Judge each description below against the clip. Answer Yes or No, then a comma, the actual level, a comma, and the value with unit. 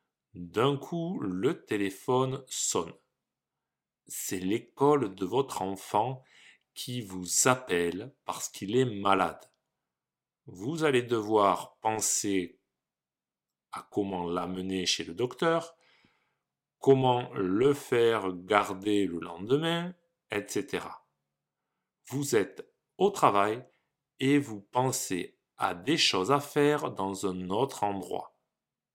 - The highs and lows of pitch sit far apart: Yes, wide, 6.1 semitones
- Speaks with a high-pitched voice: No, low, 110 Hz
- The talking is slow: Yes, slow, 105 wpm